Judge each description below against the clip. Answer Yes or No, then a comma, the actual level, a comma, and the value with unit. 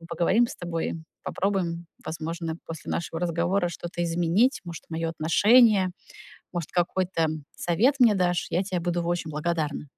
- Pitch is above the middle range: No, medium, 175 Hz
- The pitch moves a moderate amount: No, narrow, 2.1 semitones